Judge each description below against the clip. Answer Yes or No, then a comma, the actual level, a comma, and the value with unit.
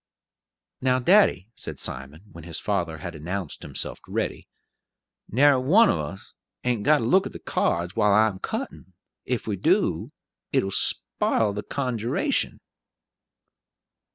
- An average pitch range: No, wide, 6.5 semitones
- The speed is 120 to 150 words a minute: Yes, average, 140 wpm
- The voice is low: Yes, low, 105 Hz